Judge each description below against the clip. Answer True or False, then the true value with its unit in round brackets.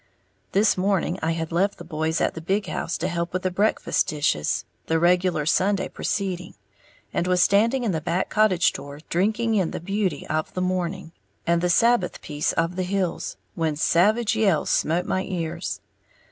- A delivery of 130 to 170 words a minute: False (180 wpm)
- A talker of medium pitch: True (180 Hz)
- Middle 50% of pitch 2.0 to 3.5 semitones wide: True (3.1 semitones)